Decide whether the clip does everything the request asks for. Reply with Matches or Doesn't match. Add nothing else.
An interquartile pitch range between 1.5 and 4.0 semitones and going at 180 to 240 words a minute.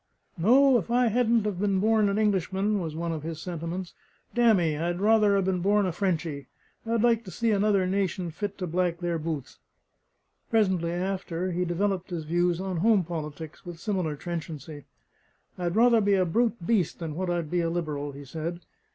Matches